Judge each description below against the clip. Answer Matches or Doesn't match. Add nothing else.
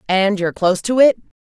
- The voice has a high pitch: Matches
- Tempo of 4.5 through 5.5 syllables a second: Doesn't match